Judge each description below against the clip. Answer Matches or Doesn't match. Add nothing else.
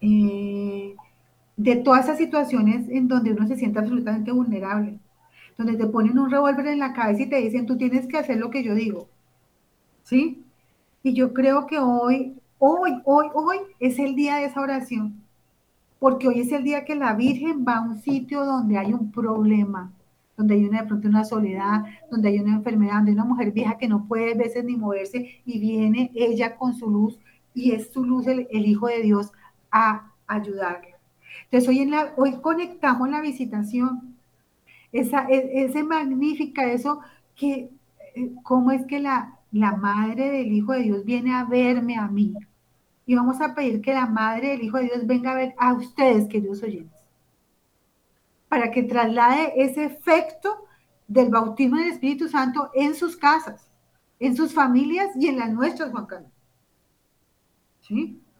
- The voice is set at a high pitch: Matches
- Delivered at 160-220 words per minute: Matches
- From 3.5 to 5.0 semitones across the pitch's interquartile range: Matches